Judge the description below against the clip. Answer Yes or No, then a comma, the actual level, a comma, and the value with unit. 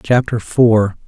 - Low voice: Yes, low, 110 Hz